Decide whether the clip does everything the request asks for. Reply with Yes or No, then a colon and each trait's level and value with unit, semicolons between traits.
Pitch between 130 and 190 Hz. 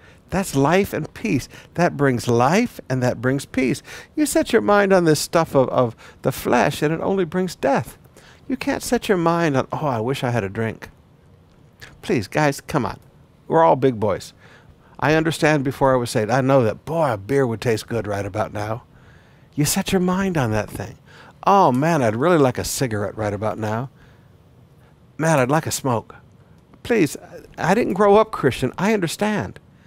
Yes: low, 135 Hz